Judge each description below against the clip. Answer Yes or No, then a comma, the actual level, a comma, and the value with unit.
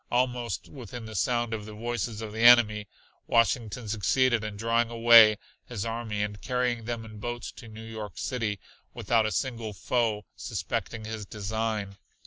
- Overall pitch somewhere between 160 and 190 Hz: No, low, 115 Hz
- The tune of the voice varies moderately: No, narrow, 1.8 semitones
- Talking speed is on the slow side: No, average, 160 wpm